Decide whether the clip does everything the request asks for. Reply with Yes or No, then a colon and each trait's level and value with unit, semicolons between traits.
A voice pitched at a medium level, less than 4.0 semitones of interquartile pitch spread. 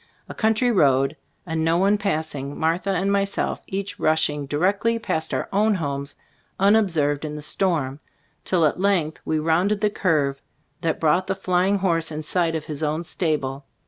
No: medium, 165 Hz; average, 4.5 semitones